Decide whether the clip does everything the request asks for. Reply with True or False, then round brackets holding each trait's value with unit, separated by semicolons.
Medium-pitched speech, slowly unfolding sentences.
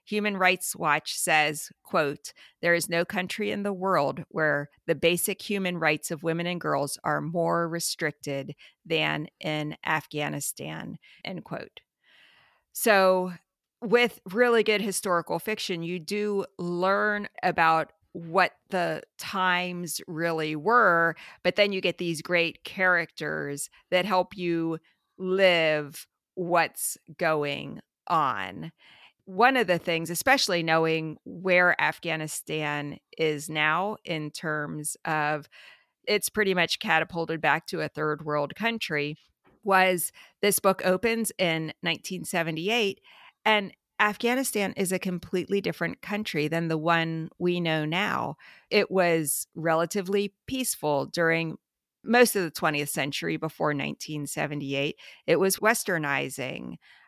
True (170 Hz; 120 wpm)